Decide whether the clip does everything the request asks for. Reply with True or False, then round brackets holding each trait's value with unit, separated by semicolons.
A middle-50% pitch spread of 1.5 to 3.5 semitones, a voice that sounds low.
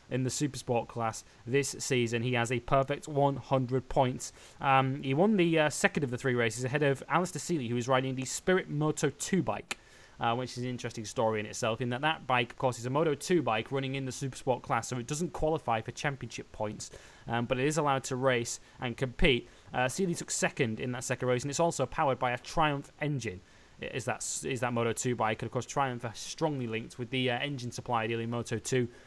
True (3.1 semitones; 130 Hz)